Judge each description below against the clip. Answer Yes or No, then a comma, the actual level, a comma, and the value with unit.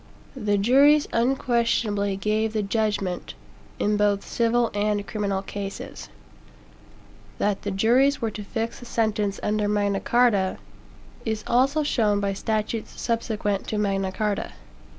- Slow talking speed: Yes, slow, 130 wpm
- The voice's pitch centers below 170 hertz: No, high, 210 Hz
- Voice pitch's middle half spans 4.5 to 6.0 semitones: No, narrow, 2.4 semitones